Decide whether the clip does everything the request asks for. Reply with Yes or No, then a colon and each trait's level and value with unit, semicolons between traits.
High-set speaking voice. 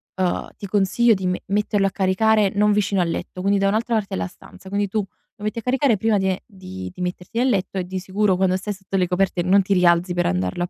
Yes: high, 195 Hz